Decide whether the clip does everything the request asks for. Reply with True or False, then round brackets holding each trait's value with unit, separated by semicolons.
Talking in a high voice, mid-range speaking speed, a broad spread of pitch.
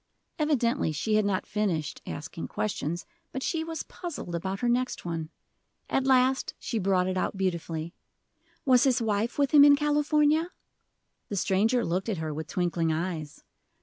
True (210 Hz; 160 wpm; 7.6 semitones)